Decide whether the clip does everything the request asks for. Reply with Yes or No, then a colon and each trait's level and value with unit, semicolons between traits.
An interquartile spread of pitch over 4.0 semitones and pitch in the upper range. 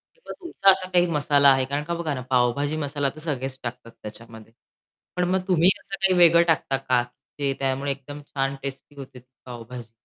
No: average, 4.6 semitones; medium, 140 Hz